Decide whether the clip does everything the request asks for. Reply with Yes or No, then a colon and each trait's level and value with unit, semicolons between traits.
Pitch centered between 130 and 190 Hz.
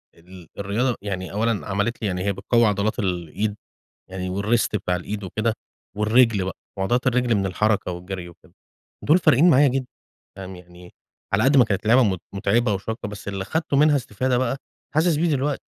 No: low, 105 Hz